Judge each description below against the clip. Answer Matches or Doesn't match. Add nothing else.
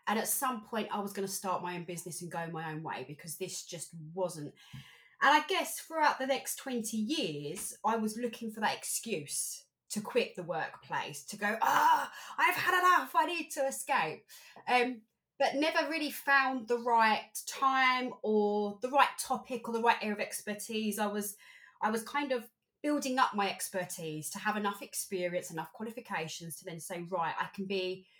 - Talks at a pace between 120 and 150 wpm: Doesn't match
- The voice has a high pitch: Matches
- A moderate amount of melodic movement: Doesn't match